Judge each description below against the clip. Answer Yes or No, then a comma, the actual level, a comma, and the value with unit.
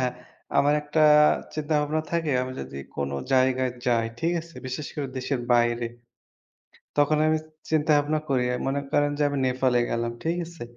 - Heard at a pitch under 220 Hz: Yes, medium, 140 Hz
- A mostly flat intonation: No, average, 3.4 semitones